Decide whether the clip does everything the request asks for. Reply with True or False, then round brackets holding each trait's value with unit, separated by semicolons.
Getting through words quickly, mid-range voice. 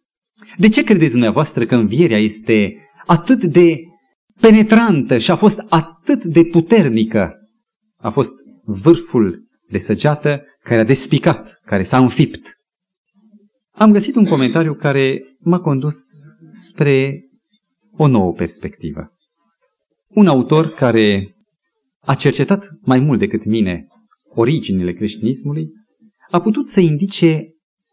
False (115 wpm; 165 Hz)